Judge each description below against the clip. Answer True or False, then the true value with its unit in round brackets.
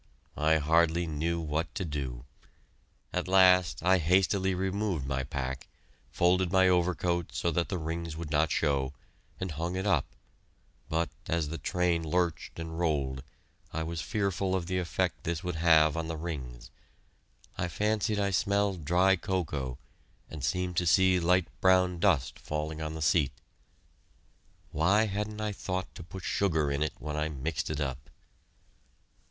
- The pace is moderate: True (160 wpm)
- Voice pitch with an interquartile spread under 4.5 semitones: True (3.2 semitones)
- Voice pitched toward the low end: True (85 Hz)